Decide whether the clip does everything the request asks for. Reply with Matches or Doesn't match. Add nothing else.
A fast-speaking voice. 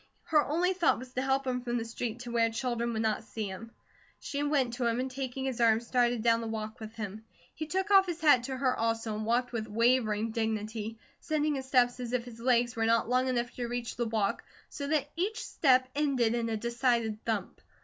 Matches